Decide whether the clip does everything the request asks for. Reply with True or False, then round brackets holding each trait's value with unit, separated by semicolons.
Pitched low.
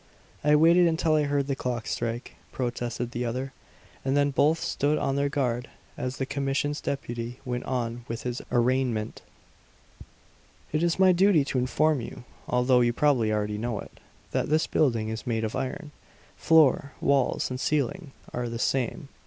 True (130 Hz)